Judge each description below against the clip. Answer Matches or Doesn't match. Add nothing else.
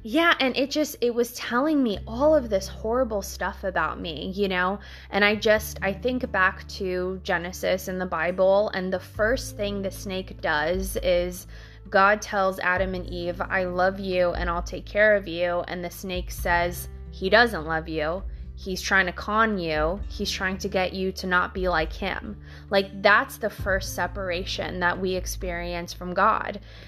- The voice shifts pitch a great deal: Doesn't match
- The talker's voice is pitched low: Doesn't match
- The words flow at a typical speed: Matches